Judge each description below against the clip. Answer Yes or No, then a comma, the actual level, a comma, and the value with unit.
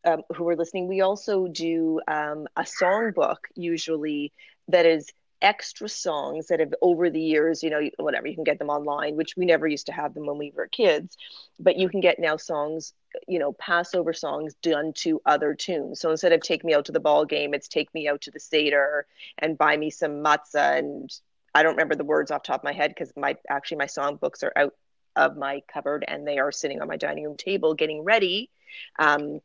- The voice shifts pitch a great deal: No, average, 2.9 semitones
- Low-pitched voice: No, medium, 155 Hz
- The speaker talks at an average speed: No, fast, 220 wpm